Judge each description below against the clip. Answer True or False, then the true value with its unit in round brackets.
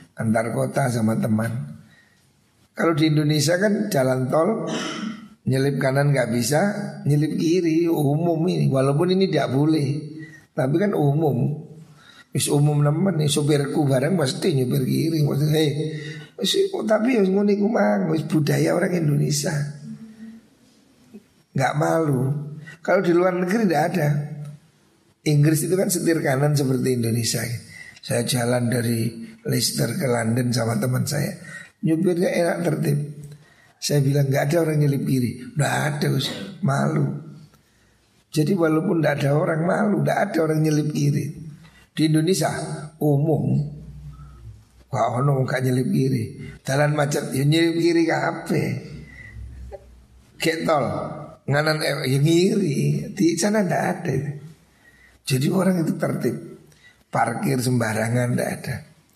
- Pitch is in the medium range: True (150 Hz)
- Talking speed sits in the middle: True (120 wpm)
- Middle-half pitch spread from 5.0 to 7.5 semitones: False (3.6 semitones)